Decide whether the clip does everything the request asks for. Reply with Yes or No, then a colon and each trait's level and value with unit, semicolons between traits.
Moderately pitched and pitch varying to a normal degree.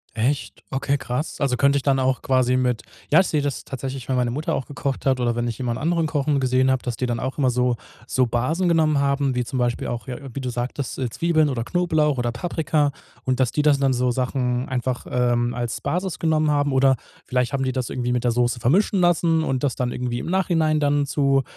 No: low, 130 Hz; average, 3.0 semitones